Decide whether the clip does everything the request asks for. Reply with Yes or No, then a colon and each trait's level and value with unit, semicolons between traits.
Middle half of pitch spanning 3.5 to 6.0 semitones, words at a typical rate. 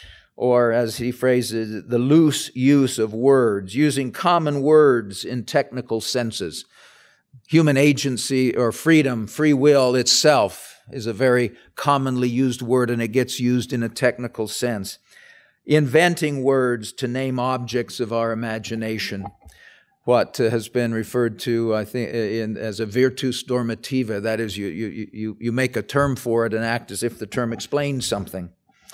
No: average, 2.7 semitones; average, 155 wpm